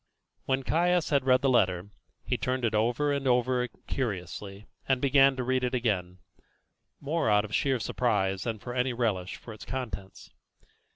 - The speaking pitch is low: Yes, low, 125 Hz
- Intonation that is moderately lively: Yes, average, 4.2 semitones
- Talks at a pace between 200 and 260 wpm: No, average, 170 wpm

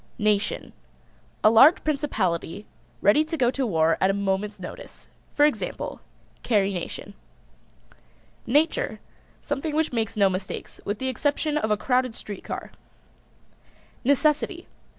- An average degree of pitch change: No, wide, 6.6 semitones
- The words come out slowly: Yes, slow, 130 wpm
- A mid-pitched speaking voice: No, high, 230 Hz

